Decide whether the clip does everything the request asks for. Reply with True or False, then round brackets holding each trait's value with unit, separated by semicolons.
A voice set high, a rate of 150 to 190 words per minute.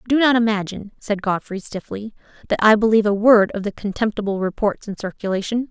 True (210 Hz; 180 wpm)